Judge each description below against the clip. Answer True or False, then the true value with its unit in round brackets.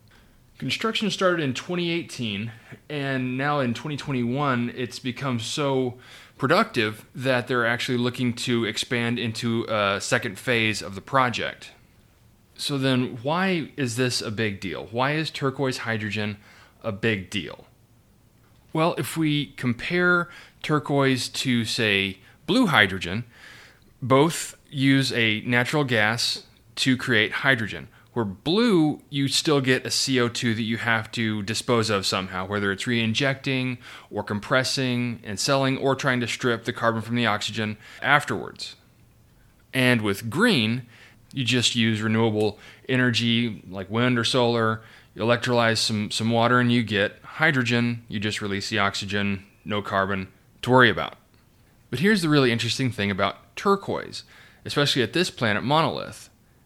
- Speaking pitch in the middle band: False (120 Hz)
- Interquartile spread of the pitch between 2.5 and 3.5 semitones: True (3.2 semitones)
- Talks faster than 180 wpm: False (140 wpm)